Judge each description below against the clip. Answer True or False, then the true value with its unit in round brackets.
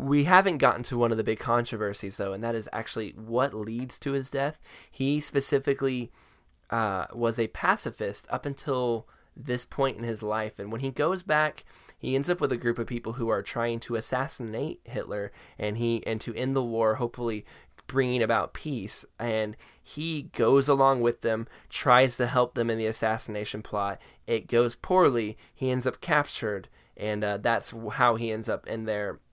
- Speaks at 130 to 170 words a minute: False (190 wpm)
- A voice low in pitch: True (120 Hz)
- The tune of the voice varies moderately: True (3.3 semitones)